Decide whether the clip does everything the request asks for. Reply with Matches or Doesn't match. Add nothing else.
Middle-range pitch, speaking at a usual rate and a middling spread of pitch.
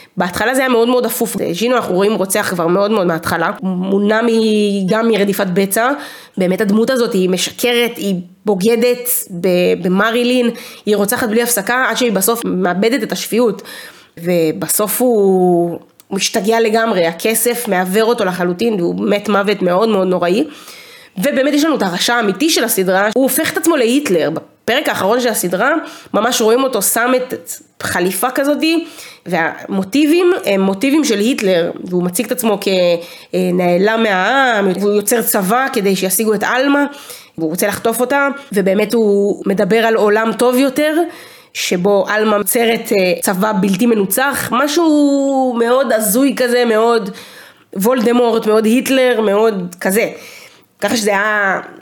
Doesn't match